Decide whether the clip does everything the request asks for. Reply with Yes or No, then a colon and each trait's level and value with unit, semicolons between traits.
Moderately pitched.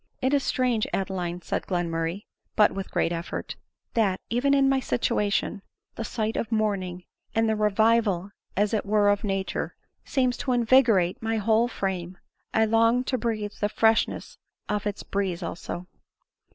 No: high, 210 Hz